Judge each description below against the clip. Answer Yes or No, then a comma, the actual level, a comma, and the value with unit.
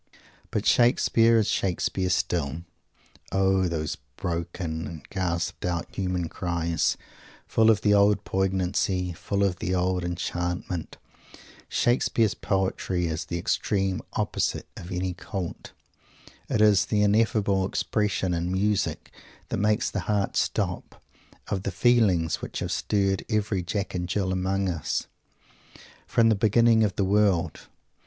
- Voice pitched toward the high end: No, very low, 95 Hz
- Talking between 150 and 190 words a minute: No, slow, 135 wpm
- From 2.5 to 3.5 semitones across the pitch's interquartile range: Yes, average, 2.8 semitones